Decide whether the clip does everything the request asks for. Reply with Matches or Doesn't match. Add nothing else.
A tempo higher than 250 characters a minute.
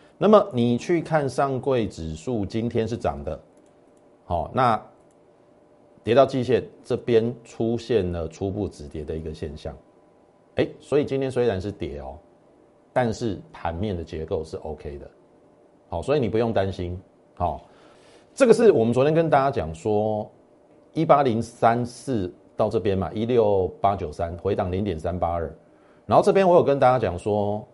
Doesn't match